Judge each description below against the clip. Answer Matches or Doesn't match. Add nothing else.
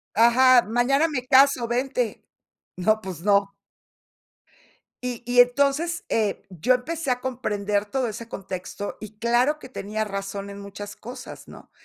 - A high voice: Matches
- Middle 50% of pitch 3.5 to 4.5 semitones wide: Matches